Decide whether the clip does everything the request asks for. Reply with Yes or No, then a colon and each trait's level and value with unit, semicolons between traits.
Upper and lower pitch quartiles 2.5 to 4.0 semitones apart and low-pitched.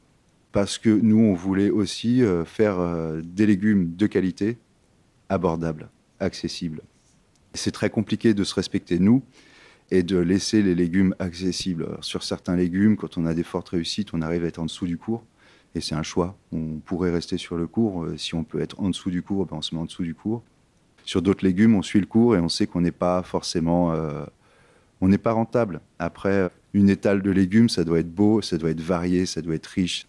Yes: average, 3.6 semitones; very low, 95 Hz